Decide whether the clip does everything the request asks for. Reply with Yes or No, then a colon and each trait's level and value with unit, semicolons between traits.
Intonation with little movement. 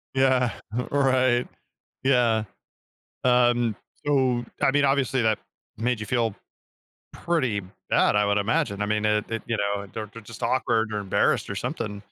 No: average, 3.3 semitones